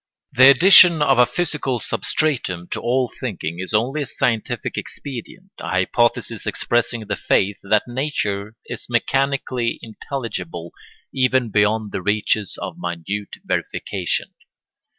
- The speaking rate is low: Yes, slow, 125 wpm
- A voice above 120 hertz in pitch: No, low, 115 Hz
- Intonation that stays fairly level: No, average, 4.6 semitones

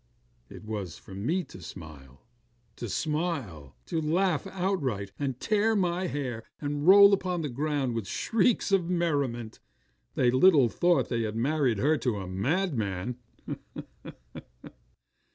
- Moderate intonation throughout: No, wide, 8.1 semitones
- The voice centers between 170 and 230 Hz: No, medium, 140 Hz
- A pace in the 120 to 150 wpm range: Yes, slow, 135 wpm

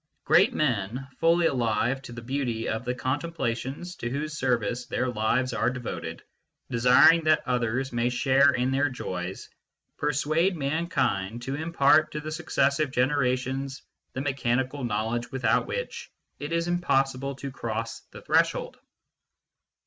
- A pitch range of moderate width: Yes, average, 3.6 semitones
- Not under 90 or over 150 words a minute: Yes, average, 140 wpm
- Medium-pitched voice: No, low, 130 Hz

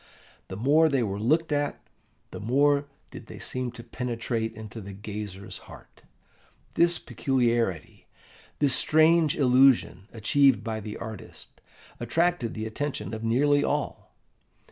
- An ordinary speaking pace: No, slow, 130 wpm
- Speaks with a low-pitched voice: Yes, low, 120 Hz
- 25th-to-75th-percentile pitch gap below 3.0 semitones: No, average, 4.7 semitones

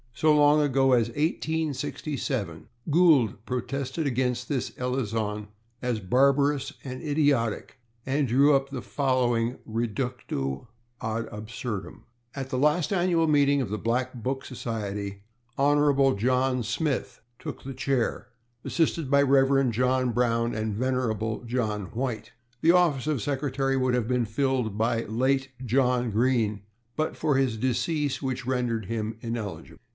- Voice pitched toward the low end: Yes, low, 130 Hz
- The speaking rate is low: Yes, slow, 130 wpm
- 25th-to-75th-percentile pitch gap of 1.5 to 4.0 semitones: Yes, average, 3.3 semitones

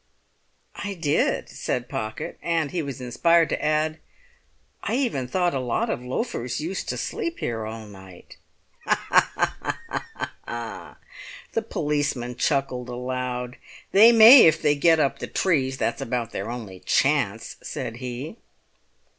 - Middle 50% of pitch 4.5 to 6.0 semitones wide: Yes, average, 5.2 semitones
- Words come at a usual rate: No, slow, 130 wpm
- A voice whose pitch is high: No, low, 135 Hz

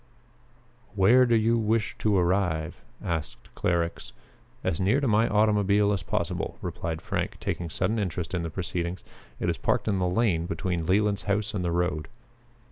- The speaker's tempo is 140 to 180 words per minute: Yes, average, 165 wpm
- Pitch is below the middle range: Yes, very low, 95 Hz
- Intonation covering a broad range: No, average, 3.4 semitones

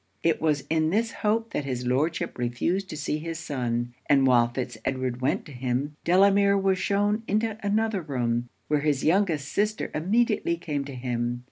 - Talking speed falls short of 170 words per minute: No, average, 175 wpm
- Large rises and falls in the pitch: Yes, wide, 7.4 semitones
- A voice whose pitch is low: No, medium, 155 Hz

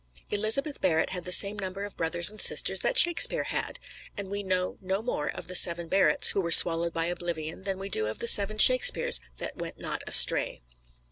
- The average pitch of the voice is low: No, high, 190 Hz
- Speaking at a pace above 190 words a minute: Yes, fast, 205 wpm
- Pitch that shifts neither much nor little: Yes, average, 3.2 semitones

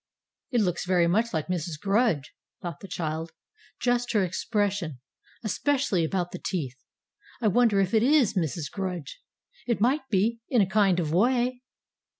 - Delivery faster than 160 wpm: No, average, 155 wpm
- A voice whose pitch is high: Yes, high, 195 Hz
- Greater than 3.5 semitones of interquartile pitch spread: Yes, average, 5.3 semitones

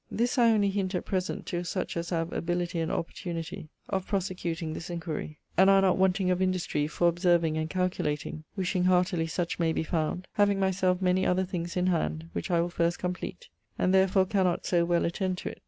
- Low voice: No, medium, 180 Hz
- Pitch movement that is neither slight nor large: No, narrow, 2.0 semitones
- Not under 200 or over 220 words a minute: Yes, fast, 205 wpm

